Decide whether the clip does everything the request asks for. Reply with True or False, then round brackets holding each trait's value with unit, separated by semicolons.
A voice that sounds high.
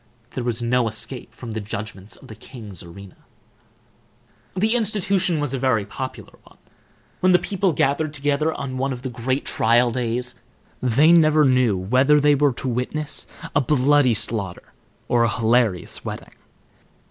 False (125 Hz)